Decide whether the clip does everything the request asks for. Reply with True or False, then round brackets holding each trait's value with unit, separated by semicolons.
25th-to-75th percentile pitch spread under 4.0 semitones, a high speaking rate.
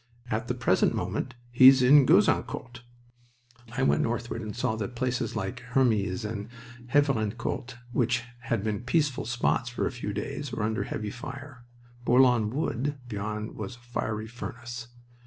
False (2.6 semitones; 150 wpm)